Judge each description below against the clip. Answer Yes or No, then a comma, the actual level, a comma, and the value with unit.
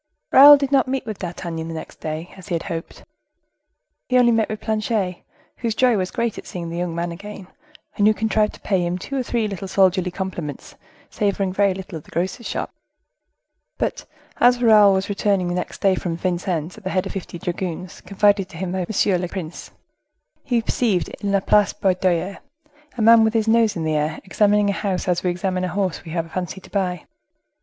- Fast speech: Yes, fast, 215 wpm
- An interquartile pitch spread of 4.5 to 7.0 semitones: No, average, 3.3 semitones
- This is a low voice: No, high, 190 Hz